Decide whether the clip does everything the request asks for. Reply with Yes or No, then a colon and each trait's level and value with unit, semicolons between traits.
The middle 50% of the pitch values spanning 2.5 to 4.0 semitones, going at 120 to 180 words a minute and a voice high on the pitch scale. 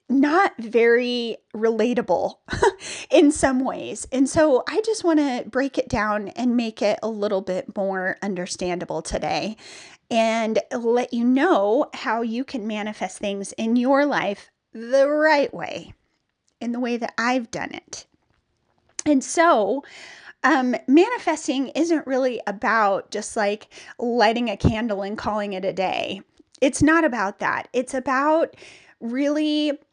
No: average, 4.9 semitones; average, 140 wpm; high, 245 Hz